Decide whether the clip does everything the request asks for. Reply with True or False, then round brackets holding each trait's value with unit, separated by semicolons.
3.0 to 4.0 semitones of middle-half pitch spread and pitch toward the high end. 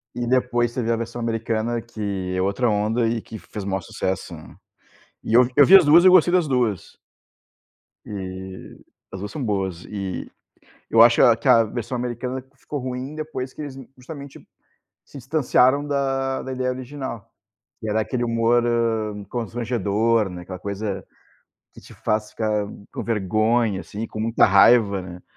False (3.6 semitones; 115 Hz)